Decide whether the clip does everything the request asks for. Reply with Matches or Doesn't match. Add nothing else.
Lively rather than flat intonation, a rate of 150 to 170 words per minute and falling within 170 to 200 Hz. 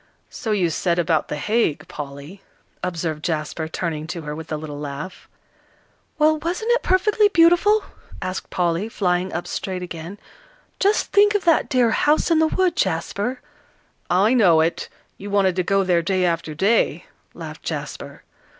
Matches